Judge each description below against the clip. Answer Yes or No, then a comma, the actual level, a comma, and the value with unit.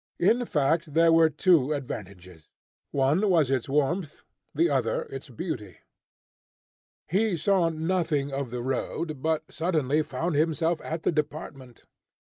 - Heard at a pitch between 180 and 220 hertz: No, medium, 155 Hz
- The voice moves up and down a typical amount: Yes, average, 3.7 semitones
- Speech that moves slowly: Yes, slow, 130 wpm